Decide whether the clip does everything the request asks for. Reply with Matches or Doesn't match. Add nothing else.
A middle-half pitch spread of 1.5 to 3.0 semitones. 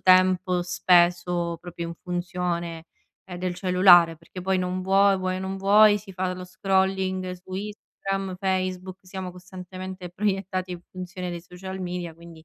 Doesn't match